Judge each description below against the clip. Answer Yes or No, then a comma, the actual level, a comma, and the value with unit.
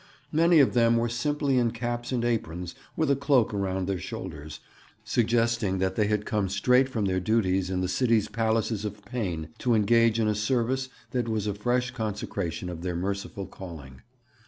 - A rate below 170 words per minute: No, average, 180 wpm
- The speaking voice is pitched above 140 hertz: No, low, 110 Hz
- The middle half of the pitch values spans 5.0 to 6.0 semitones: No, average, 4.1 semitones